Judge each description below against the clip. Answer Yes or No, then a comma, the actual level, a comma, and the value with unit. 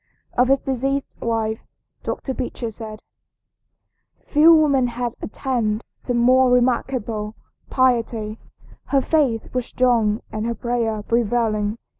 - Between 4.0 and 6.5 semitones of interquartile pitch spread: No, narrow, 2.6 semitones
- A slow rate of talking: Yes, slow, 115 wpm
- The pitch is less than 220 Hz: No, high, 240 Hz